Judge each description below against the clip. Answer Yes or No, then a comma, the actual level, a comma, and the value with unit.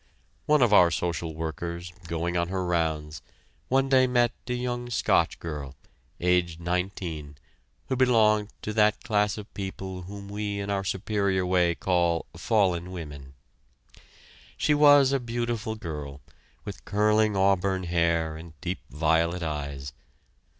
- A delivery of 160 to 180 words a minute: No, slow, 135 wpm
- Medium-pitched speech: No, very low, 90 Hz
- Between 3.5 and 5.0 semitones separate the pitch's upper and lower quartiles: Yes, average, 4.3 semitones